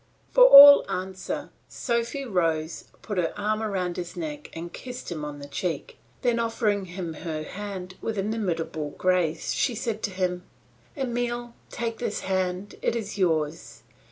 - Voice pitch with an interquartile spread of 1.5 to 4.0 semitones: No, average, 5.1 semitones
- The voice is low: No, high, 195 Hz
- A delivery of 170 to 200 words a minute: No, average, 155 wpm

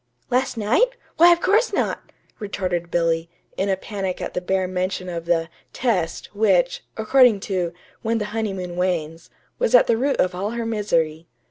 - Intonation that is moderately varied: Yes, average, 4.4 semitones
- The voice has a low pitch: No, high, 190 Hz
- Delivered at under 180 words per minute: Yes, average, 170 wpm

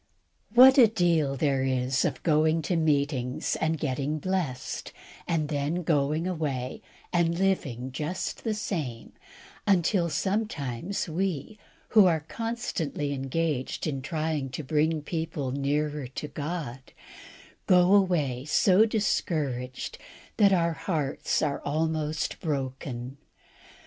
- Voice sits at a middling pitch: Yes, medium, 155 Hz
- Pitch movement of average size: Yes, average, 4.2 semitones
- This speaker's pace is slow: Yes, slow, 115 wpm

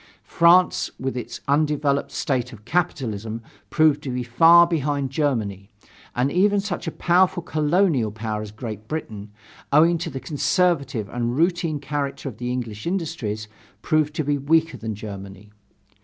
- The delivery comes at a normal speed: Yes, average, 150 wpm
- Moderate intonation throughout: No, wide, 6.3 semitones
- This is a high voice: No, medium, 140 Hz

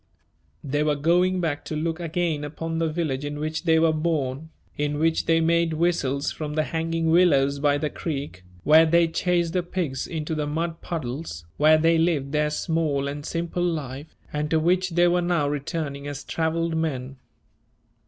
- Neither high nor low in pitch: Yes, medium, 160 Hz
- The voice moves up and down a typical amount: No, narrow, 2.3 semitones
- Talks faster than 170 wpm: Yes, average, 180 wpm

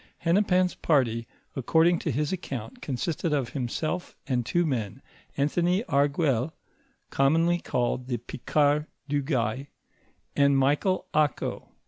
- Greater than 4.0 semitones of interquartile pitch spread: Yes, average, 4.4 semitones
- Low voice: No, medium, 145 Hz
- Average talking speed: No, slow, 120 wpm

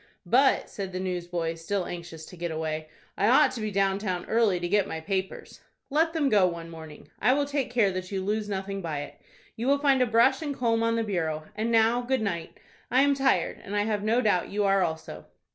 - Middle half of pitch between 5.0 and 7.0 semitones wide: Yes, average, 5.3 semitones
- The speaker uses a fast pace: Yes, fast, 230 wpm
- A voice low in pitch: No, high, 205 Hz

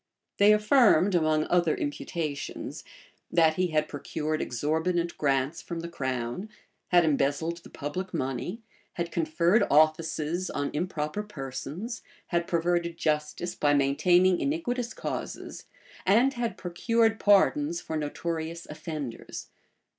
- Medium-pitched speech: Yes, medium, 170 Hz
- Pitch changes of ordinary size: Yes, average, 3.6 semitones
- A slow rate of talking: Yes, slow, 115 wpm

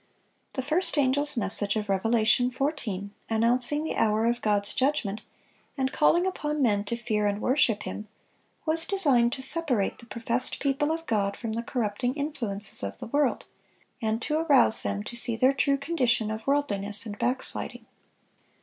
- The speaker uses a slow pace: No, average, 165 wpm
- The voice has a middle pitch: No, high, 240 Hz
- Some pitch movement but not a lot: Yes, average, 5.0 semitones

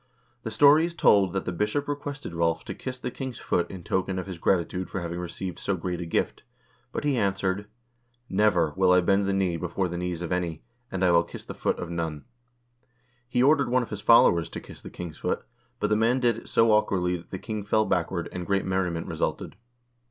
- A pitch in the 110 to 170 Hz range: No, very low, 95 Hz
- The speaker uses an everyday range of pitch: Yes, average, 4.2 semitones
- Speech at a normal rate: No, fast, 225 wpm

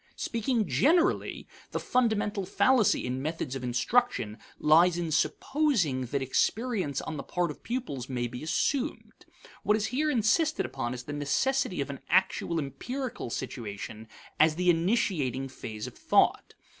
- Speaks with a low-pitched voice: No, medium, 170 Hz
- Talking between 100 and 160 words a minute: Yes, average, 145 wpm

